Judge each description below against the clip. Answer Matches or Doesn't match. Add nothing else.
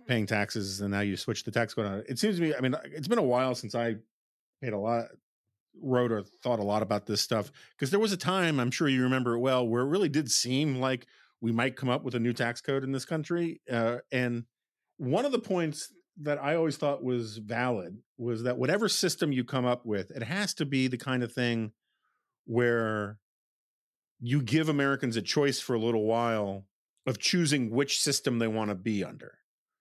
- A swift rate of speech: Matches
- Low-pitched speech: Matches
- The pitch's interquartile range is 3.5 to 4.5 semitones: Matches